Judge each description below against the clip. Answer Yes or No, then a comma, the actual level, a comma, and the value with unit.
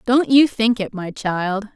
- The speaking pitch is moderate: No, high, 220 Hz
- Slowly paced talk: No, fast, 205 wpm